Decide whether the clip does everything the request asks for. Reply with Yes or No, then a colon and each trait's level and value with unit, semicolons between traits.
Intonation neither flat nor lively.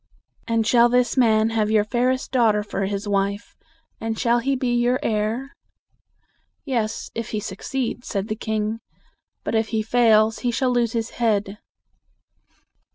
No: narrow, 2.1 semitones